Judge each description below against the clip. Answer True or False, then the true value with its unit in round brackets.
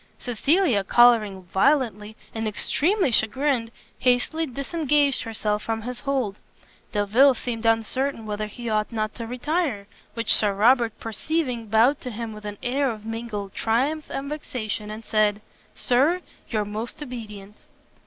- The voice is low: False (230 Hz)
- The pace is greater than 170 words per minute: False (140 wpm)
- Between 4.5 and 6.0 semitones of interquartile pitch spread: False (4.1 semitones)